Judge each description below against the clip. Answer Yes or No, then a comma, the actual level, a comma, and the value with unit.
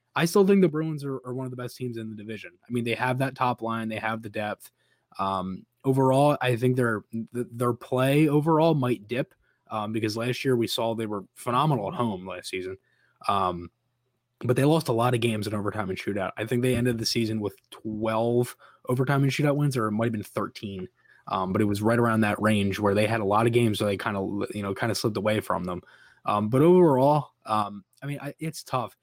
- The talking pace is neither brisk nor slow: No, fast, 240 wpm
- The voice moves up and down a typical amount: Yes, average, 3.4 semitones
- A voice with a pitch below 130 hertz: Yes, low, 115 Hz